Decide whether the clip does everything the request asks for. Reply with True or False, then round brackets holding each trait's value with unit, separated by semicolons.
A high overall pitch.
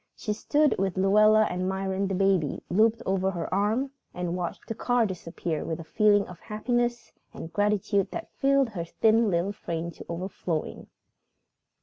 True (195 Hz)